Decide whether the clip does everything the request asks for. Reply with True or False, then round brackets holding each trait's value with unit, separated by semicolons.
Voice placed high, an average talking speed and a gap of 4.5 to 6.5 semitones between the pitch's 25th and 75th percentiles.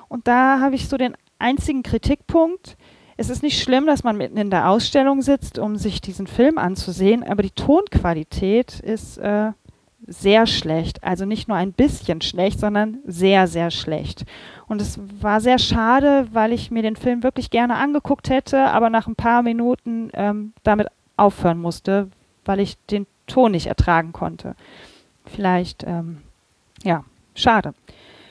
True (215 Hz; 160 wpm; 4.8 semitones)